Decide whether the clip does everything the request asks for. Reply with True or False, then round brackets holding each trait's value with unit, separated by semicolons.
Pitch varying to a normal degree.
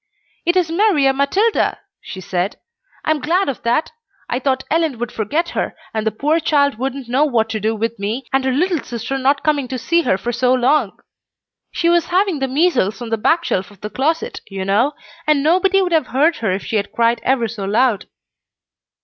False (6.0 semitones)